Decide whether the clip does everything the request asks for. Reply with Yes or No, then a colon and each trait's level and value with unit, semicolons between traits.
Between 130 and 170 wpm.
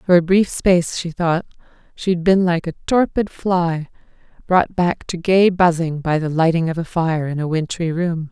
No: average, 200 wpm